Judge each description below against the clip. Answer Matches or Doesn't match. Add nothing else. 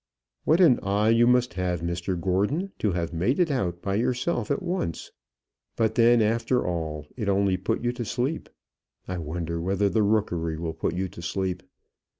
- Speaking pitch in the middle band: Doesn't match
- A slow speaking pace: Doesn't match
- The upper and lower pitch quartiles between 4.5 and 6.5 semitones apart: Matches